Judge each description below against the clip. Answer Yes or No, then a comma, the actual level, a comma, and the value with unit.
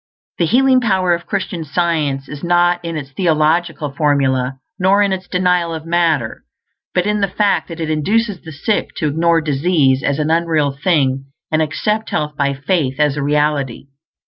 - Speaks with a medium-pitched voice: Yes, medium, 160 Hz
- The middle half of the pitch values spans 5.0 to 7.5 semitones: No, average, 3.8 semitones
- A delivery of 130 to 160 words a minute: No, average, 175 wpm